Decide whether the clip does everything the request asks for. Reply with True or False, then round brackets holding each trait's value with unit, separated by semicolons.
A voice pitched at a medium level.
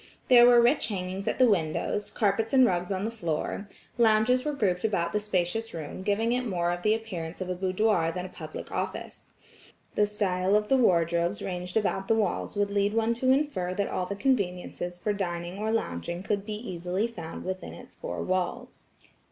False (200 Hz)